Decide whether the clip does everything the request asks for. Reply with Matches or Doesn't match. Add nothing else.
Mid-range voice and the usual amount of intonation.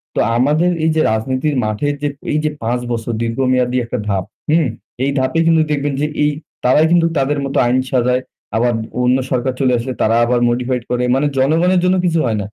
Doesn't match